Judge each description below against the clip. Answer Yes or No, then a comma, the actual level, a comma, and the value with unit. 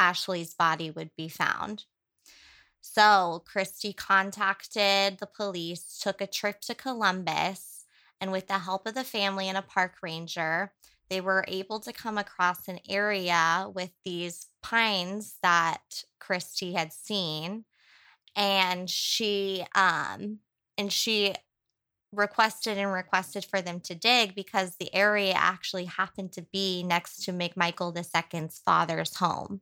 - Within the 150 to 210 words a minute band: No, slow, 135 wpm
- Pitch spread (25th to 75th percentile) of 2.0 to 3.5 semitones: Yes, narrow, 2.5 semitones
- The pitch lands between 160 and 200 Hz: Yes, high, 190 Hz